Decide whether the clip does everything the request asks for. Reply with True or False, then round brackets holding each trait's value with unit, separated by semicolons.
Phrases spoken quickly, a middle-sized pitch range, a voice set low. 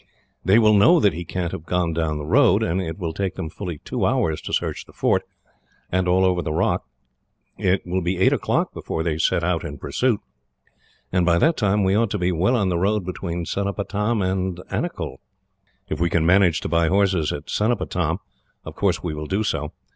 True (210 wpm; 3.0 semitones; 90 Hz)